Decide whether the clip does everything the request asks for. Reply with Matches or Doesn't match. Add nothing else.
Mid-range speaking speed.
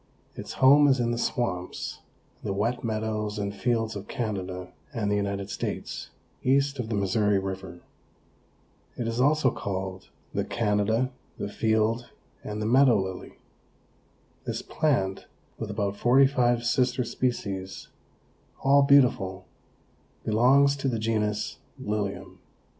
Doesn't match